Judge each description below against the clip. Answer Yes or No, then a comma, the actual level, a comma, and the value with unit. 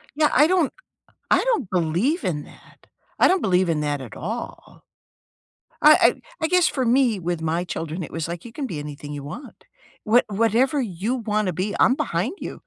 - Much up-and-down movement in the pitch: Yes, wide, 7.8 semitones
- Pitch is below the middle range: No, high, 200 Hz